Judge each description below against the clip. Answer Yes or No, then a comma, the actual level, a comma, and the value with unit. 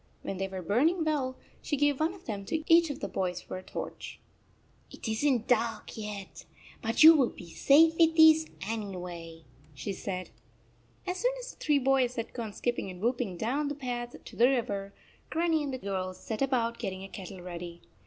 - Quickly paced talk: Yes, fast, 215 wpm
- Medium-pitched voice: No, high, 235 Hz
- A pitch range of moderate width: No, wide, 7.0 semitones